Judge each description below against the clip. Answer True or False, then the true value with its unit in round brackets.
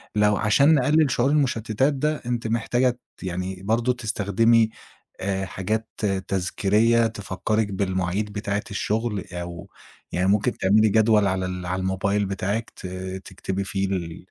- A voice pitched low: True (105 Hz)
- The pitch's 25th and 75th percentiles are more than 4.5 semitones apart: False (3.3 semitones)